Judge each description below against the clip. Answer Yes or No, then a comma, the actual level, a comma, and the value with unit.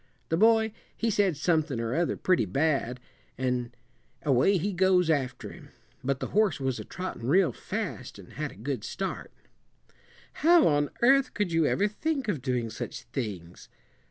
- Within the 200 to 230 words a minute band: No, average, 165 wpm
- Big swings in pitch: Yes, wide, 7.8 semitones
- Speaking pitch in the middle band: Yes, medium, 160 Hz